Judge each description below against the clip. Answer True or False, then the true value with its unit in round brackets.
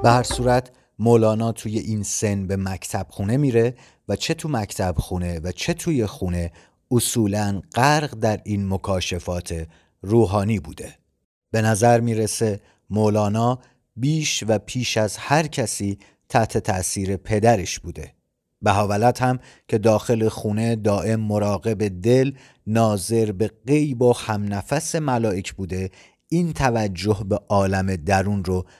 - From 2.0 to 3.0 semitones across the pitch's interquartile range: False (3.5 semitones)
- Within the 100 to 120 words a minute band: False (130 wpm)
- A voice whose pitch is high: False (110 Hz)